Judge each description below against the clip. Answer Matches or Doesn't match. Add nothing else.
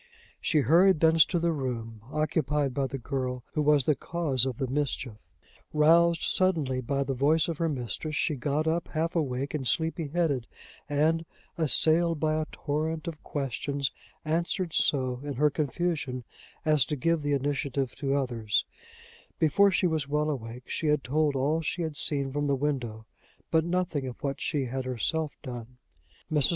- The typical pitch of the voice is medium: Matches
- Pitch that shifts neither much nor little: Matches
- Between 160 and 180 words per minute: Matches